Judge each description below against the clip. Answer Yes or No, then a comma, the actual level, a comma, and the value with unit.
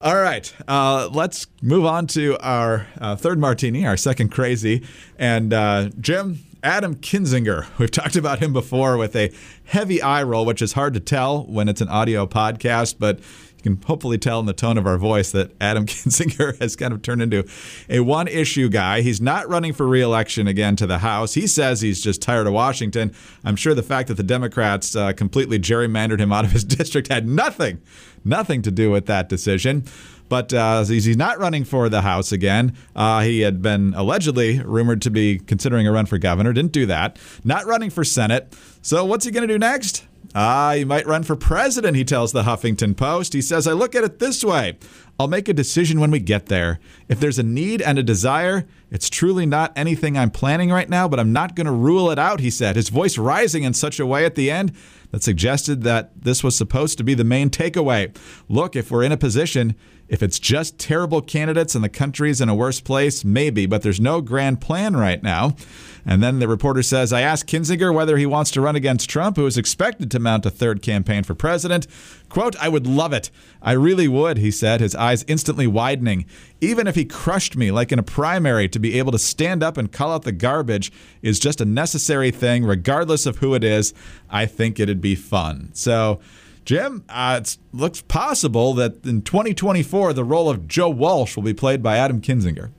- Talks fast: Yes, fast, 215 wpm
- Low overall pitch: Yes, low, 125 Hz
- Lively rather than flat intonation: Yes, wide, 5.8 semitones